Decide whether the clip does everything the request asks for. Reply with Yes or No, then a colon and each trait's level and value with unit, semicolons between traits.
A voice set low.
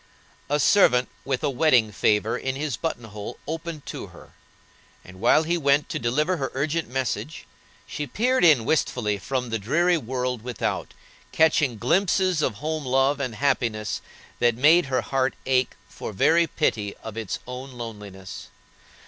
Yes: low, 130 Hz